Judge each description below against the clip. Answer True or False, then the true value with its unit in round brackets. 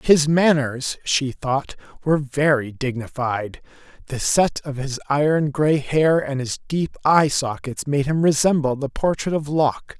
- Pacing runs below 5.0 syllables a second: True (4.2 syllables/s)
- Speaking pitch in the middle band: True (145 Hz)